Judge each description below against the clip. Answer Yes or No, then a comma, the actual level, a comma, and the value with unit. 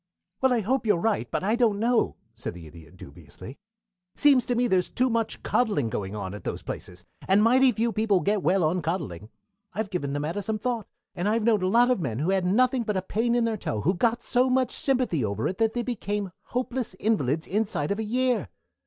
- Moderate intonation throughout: No, wide, 6.8 semitones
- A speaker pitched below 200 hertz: No, high, 210 Hz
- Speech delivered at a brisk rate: Yes, fast, 230 wpm